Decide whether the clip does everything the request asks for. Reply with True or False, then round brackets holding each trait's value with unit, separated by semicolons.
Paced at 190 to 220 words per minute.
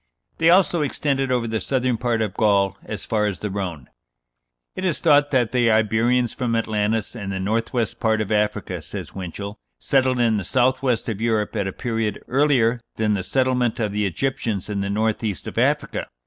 True (200 wpm)